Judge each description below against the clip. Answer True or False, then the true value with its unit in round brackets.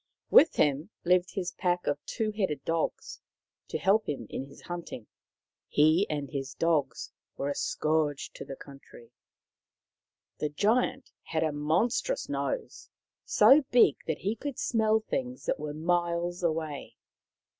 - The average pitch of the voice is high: False (170 Hz)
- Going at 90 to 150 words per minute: True (145 wpm)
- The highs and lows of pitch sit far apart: True (6.3 semitones)